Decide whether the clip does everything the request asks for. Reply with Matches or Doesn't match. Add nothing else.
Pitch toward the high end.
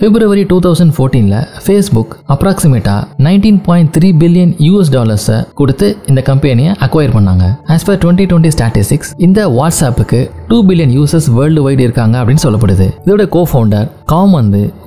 Doesn't match